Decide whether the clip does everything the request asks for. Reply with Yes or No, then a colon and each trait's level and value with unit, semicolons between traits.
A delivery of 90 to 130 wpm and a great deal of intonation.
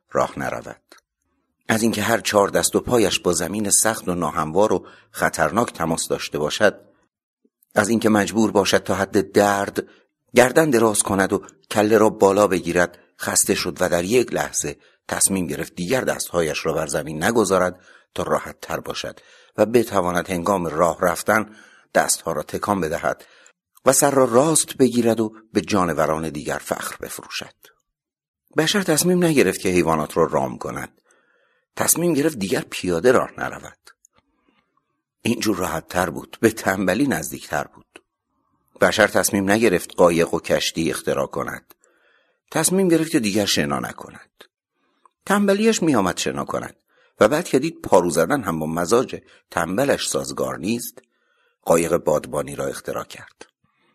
No: average, 145 wpm; wide, 6.1 semitones